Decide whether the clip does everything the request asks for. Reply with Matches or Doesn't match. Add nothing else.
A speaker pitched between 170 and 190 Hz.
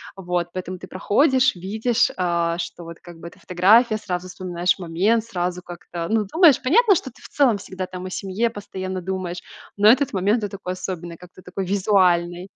Matches